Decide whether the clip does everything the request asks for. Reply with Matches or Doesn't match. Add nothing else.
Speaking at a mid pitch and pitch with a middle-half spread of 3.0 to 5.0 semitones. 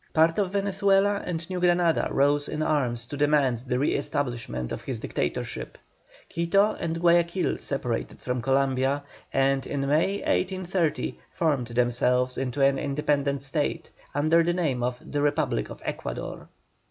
Matches